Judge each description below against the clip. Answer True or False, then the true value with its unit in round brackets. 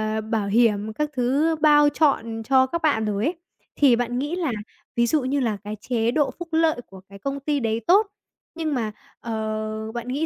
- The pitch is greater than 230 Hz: True (245 Hz)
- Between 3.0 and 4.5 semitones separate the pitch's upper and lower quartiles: False (5.1 semitones)